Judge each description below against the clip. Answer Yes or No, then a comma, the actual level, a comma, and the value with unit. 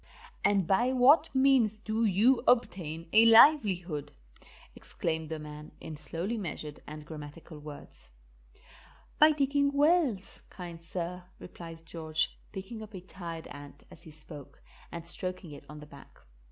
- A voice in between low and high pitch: Yes, medium, 175 Hz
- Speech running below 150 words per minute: Yes, average, 140 wpm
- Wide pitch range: Yes, wide, 6.2 semitones